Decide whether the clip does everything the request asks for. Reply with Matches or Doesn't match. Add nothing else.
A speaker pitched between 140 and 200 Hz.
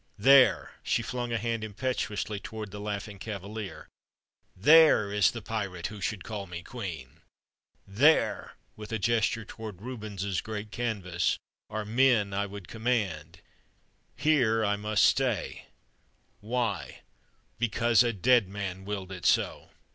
Doesn't match